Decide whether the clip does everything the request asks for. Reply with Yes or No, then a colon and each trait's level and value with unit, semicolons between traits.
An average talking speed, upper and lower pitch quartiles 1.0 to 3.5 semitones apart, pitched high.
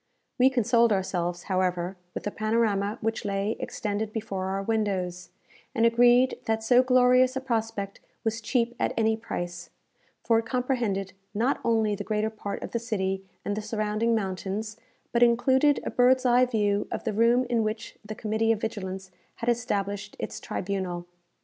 Yes: average, 165 wpm; average, 2.9 semitones; high, 220 Hz